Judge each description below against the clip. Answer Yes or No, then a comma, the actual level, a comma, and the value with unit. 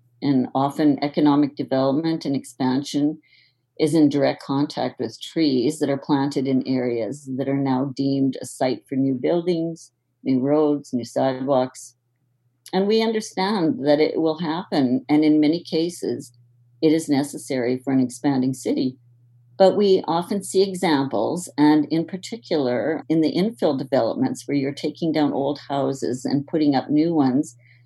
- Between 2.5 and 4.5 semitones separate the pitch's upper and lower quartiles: Yes, average, 3.3 semitones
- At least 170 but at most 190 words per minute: No, average, 155 wpm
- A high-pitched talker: No, medium, 140 Hz